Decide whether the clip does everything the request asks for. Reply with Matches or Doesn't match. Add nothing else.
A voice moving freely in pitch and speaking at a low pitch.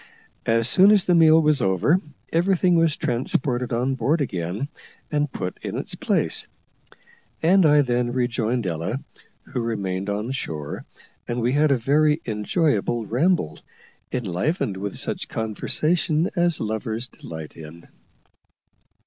Matches